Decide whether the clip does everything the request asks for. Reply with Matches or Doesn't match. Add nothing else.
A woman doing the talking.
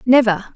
Matches